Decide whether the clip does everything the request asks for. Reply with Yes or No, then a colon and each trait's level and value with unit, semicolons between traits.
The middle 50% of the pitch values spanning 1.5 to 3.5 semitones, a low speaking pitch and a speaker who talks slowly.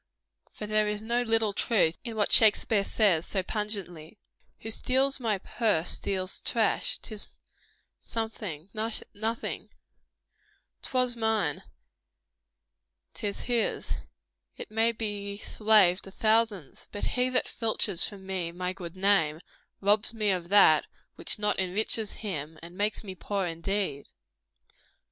No: average, 3.1 semitones; high, 205 Hz; slow, 130 wpm